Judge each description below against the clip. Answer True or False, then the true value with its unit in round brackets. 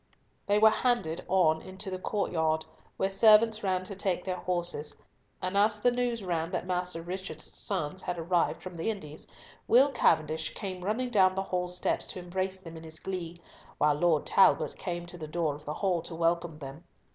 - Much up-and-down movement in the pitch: False (2.9 semitones)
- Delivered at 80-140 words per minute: False (190 wpm)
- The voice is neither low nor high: True (180 Hz)